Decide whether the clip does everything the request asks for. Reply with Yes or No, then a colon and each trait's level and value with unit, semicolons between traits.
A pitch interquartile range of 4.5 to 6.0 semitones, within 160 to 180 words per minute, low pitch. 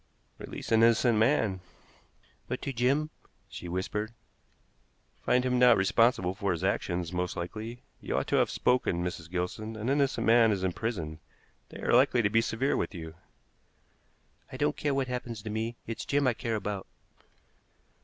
Yes: average, 4.9 semitones; average, 170 wpm; low, 110 Hz